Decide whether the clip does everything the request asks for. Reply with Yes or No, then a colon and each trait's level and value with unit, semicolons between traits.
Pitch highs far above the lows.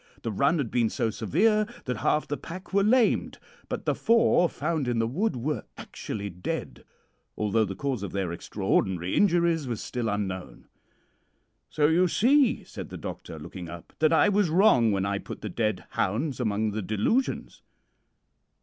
Yes: wide, 8.9 semitones